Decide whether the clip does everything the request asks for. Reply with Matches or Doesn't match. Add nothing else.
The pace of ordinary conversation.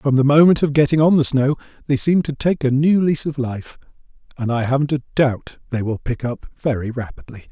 Doesn't match